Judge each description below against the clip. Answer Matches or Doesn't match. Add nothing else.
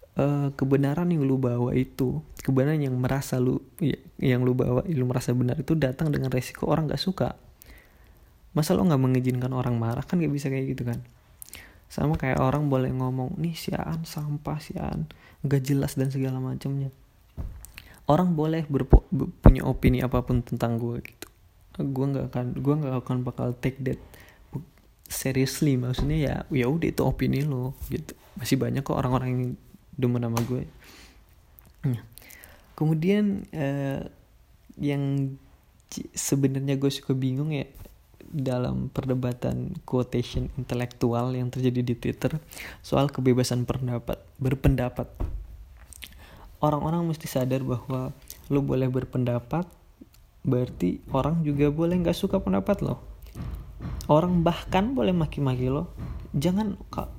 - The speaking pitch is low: Matches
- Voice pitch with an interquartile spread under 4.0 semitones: Matches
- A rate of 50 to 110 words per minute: Doesn't match